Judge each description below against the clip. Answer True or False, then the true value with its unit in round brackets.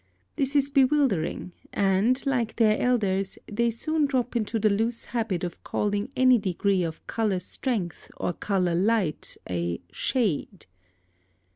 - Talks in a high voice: True (215 Hz)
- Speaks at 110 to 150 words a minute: True (135 wpm)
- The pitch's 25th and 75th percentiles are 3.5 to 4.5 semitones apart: False (4.9 semitones)